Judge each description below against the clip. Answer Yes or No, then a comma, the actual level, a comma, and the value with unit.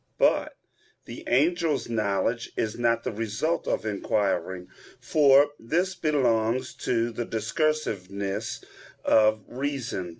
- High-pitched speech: No, low, 115 Hz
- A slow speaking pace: Yes, slow, 105 wpm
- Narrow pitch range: No, average, 4.9 semitones